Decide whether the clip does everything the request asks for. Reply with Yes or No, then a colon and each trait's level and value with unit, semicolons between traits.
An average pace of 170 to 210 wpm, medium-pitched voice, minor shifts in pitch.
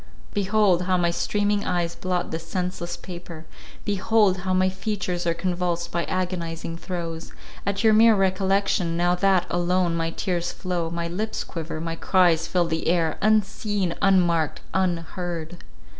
No: average, 145 wpm; medium, 180 Hz; narrow, 2.2 semitones